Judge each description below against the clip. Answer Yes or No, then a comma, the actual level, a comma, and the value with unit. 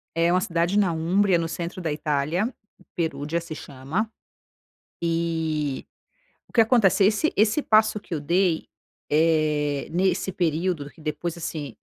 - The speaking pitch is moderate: Yes, medium, 170 Hz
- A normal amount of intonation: Yes, average, 3.7 semitones